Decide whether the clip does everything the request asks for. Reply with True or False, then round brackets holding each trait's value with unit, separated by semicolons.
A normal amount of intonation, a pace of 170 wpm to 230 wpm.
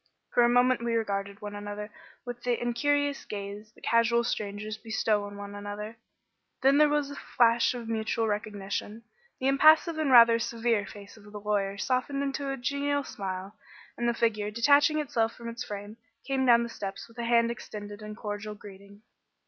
True (3.1 semitones; 180 wpm)